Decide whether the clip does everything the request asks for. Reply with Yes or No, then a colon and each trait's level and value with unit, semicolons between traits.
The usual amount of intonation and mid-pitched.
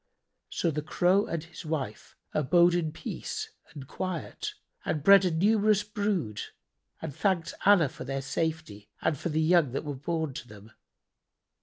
Yes: average, 4.6 semitones; medium, 160 Hz